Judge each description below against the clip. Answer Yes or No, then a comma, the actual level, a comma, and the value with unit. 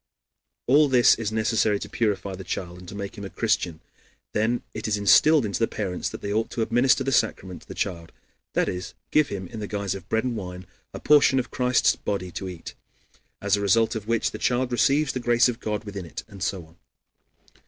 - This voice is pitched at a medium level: No, low, 105 Hz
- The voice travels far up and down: No, average, 3.9 semitones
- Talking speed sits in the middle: No, fast, 225 wpm